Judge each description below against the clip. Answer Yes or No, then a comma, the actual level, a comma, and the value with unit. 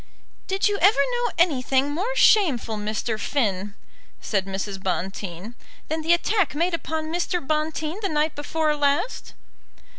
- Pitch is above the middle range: Yes, very high, 300 Hz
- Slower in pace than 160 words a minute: Yes, average, 140 wpm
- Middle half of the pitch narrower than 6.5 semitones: No, wide, 7.9 semitones